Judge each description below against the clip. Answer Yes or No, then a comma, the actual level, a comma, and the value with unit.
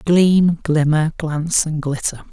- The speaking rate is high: No, slow, 130 wpm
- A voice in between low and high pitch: Yes, medium, 160 Hz